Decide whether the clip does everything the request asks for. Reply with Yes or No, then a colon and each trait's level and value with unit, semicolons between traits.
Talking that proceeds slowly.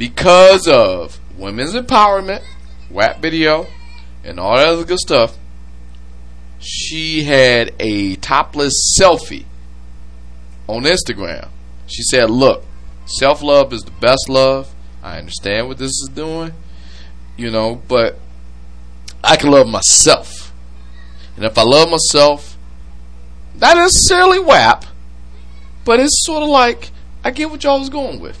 Yes: slow, 130 wpm